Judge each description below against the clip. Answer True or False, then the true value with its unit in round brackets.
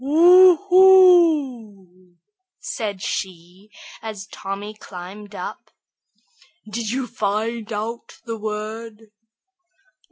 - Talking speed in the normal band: False (85 wpm)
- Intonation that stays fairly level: False (4.2 semitones)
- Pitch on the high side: True (215 Hz)